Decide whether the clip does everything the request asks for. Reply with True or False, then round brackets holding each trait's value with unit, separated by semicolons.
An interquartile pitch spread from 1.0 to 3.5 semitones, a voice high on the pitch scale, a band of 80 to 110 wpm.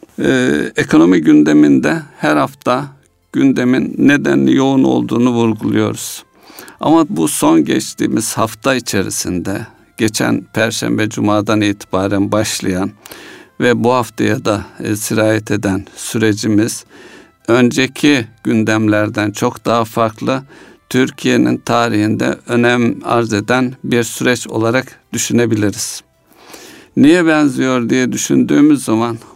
False (3.1 semitones; 115 Hz; 95 wpm)